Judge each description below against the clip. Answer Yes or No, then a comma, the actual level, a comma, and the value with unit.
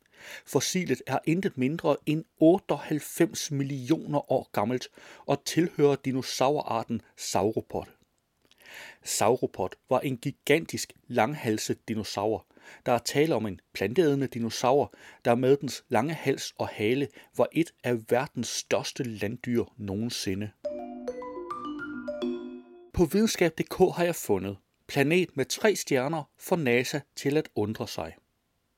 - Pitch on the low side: Yes, low, 130 Hz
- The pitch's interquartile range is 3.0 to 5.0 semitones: No, wide, 5.4 semitones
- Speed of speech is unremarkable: No, slow, 115 wpm